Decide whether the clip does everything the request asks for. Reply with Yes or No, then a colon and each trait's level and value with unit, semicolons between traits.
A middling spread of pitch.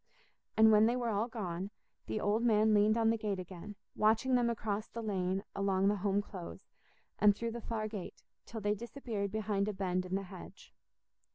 No: narrow, 2.2 semitones